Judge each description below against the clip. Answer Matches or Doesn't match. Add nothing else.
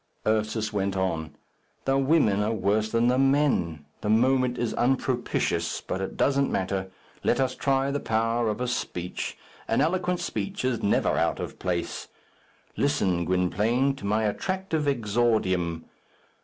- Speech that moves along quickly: Doesn't match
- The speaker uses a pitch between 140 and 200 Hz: Doesn't match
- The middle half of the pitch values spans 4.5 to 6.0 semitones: Matches